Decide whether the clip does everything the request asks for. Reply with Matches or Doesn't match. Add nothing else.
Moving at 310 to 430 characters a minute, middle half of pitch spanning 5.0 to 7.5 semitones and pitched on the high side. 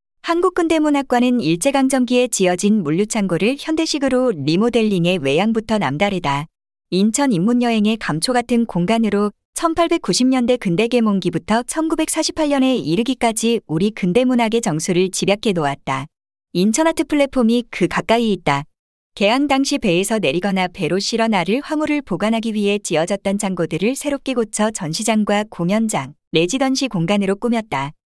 Matches